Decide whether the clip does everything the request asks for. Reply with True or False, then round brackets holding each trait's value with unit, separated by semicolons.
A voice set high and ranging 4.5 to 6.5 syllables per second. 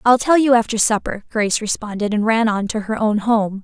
True (220 Hz; 5.5 syllables/s)